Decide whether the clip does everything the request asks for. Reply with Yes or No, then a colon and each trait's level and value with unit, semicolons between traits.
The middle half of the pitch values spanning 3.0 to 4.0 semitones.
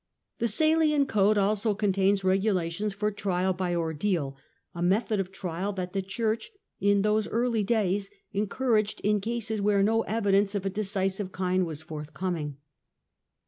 No: narrow, 2.4 semitones